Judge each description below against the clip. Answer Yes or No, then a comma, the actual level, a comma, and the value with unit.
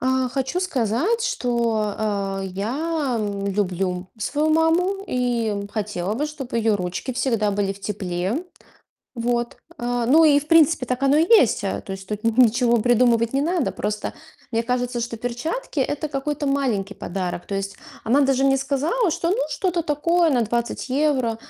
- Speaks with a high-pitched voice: Yes, high, 245 Hz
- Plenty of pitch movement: Yes, wide, 5.7 semitones